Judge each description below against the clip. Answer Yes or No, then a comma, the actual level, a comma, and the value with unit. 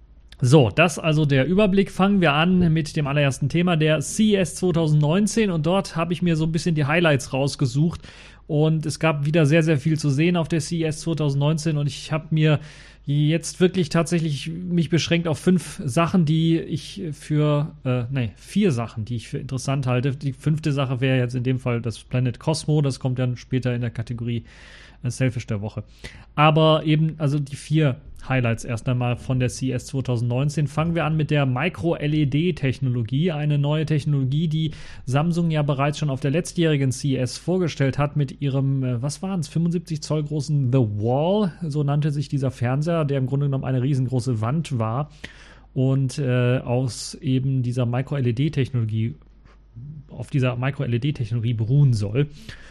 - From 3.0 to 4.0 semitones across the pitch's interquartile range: Yes, average, 3.7 semitones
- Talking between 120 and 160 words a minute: No, average, 170 wpm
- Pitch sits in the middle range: Yes, medium, 145 Hz